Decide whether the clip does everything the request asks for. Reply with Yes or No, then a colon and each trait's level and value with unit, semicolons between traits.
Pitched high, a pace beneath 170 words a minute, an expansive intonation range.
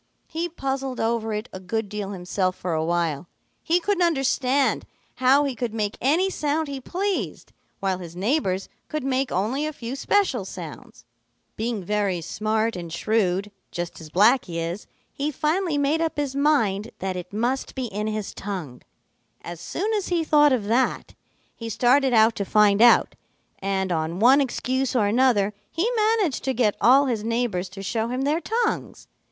No: high, 230 Hz; average, 175 wpm; wide, 6.2 semitones